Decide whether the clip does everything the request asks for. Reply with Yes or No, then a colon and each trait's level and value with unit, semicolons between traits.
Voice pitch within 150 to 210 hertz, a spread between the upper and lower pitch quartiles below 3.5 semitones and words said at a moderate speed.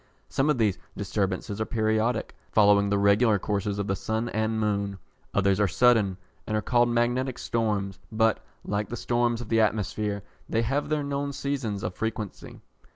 No: low, 110 Hz; average, 2.8 semitones; average, 170 wpm